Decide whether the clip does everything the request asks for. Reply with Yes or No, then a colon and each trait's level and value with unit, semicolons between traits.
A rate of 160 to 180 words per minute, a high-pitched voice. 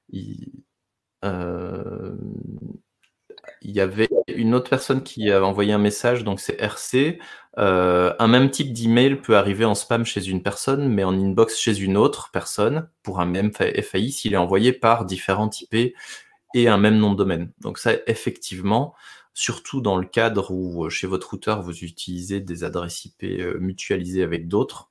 No: average, 170 wpm; low, 105 Hz